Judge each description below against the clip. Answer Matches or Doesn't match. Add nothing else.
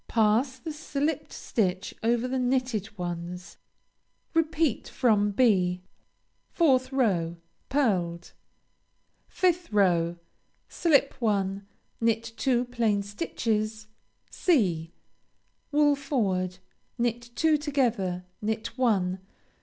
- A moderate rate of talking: Doesn't match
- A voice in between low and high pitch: Doesn't match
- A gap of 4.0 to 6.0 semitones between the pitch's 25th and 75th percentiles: Matches